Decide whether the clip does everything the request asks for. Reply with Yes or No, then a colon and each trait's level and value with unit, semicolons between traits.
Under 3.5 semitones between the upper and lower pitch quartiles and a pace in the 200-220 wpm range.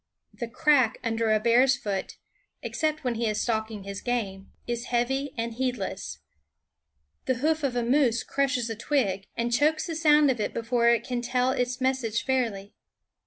No: average, 2.7 semitones; average, 180 wpm